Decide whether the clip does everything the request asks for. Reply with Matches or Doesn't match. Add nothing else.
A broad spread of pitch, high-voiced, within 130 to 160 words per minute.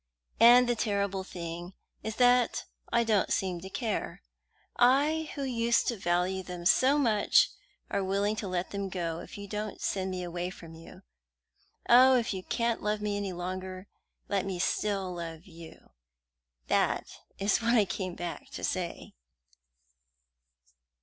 Doesn't match